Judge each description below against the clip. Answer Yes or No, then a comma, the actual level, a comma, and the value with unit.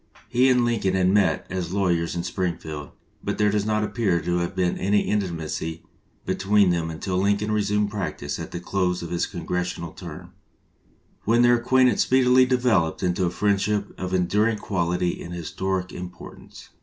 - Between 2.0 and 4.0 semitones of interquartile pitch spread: Yes, average, 3.2 semitones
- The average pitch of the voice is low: Yes, very low, 95 Hz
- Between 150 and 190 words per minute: Yes, average, 170 wpm